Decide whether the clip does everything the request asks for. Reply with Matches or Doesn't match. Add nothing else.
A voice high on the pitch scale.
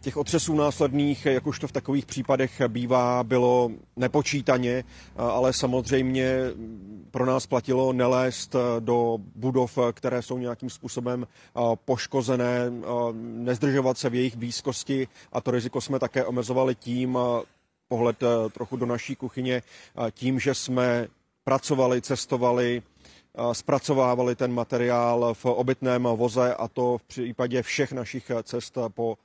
Doesn't match